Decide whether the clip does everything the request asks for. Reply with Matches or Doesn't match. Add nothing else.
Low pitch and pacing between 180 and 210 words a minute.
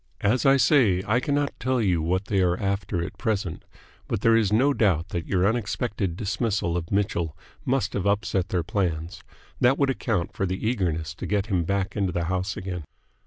Matches